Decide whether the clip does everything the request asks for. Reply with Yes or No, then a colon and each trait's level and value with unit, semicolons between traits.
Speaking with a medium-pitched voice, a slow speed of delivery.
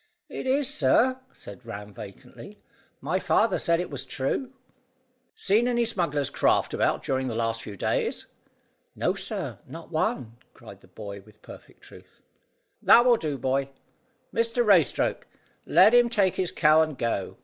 No: medium, 155 Hz; average, 155 wpm